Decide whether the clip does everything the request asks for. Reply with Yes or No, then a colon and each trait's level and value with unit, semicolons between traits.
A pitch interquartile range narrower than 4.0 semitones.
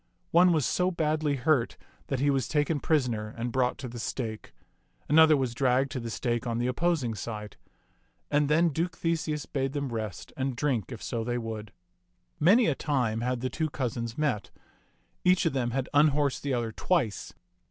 No: average, 4.4 semitones